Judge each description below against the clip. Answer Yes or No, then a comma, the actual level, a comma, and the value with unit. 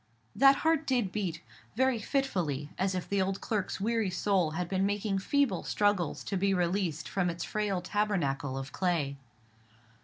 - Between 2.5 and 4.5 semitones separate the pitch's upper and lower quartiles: Yes, average, 3.3 semitones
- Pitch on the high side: Yes, high, 195 Hz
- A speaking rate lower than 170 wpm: Yes, average, 160 wpm